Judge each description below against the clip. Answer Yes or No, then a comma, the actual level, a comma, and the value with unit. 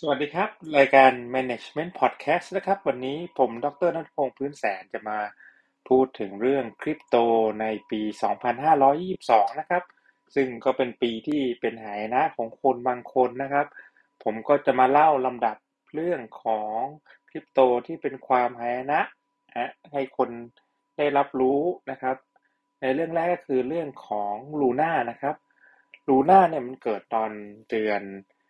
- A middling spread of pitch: Yes, average, 3.7 semitones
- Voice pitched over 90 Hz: Yes, low, 130 Hz